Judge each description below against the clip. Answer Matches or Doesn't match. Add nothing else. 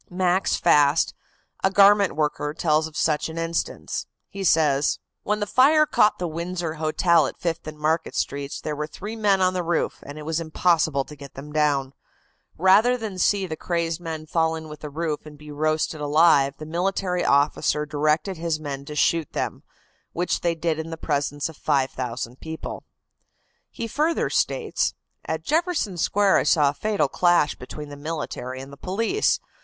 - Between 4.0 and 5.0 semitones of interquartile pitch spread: Doesn't match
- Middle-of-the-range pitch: Matches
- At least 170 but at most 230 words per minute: Matches